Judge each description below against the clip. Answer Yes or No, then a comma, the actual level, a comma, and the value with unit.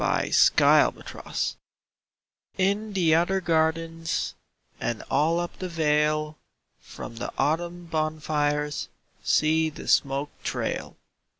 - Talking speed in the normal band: No, slow, 105 wpm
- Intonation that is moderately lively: No, narrow, 2.1 semitones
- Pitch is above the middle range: No, medium, 160 Hz